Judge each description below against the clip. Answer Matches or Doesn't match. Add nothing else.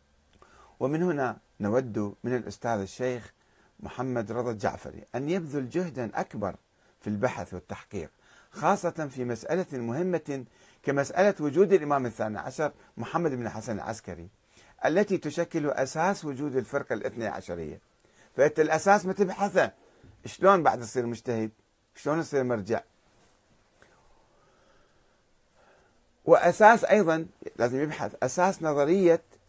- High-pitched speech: Doesn't match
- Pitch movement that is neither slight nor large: Doesn't match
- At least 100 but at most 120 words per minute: Matches